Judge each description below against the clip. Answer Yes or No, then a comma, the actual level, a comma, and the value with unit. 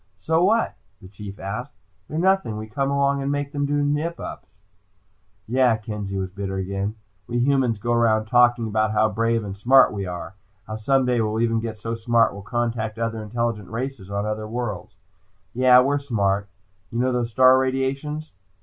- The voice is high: No, low, 115 Hz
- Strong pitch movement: No, average, 3.8 semitones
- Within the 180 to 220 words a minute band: Yes, average, 185 wpm